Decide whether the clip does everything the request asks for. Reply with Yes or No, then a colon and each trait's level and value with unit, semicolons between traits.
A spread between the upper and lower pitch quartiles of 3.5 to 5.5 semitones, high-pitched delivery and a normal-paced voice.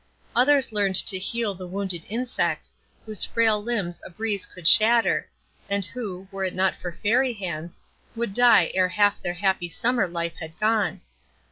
Yes: average, 3.8 semitones; high, 200 Hz; average, 165 wpm